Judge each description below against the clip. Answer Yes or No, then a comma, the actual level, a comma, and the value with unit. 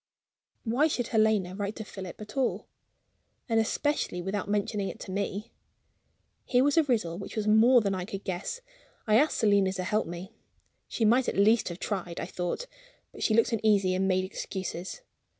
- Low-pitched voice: No, high, 210 Hz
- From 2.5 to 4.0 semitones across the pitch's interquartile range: Yes, average, 3.3 semitones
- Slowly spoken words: No, average, 185 wpm